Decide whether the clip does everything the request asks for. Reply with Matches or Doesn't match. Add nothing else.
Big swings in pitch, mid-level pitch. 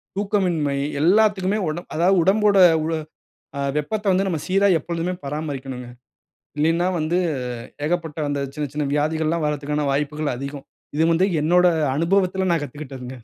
Doesn't match